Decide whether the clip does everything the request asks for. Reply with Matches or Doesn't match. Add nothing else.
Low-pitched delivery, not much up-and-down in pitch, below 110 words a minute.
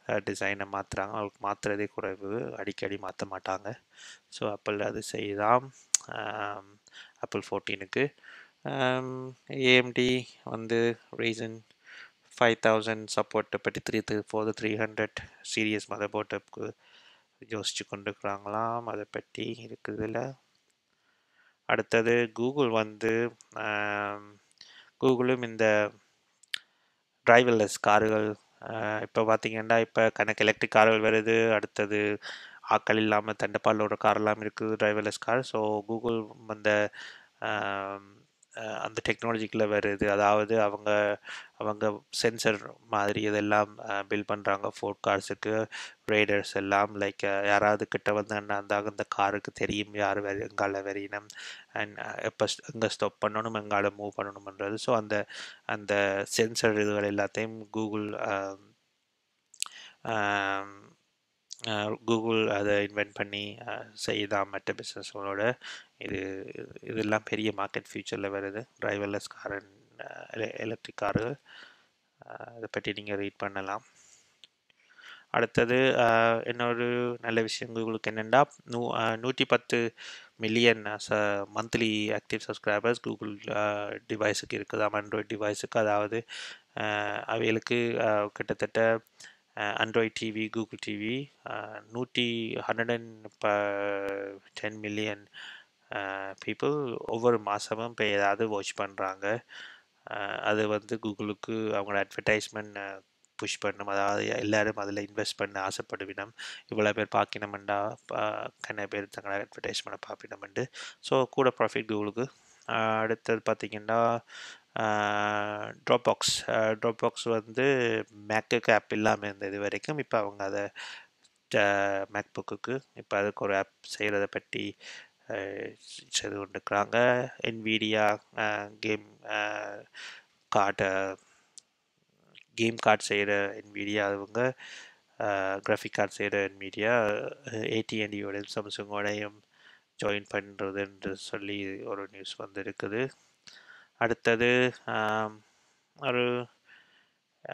Matches